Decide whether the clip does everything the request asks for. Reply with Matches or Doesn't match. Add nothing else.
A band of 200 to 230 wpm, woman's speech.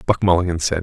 Doesn't match